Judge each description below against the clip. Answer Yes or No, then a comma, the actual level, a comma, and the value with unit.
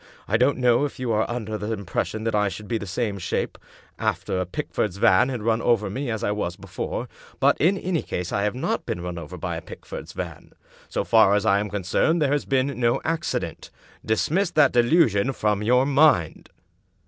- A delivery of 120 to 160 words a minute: No, fast, 205 wpm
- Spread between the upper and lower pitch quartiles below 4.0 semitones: No, average, 4.7 semitones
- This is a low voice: Yes, low, 110 Hz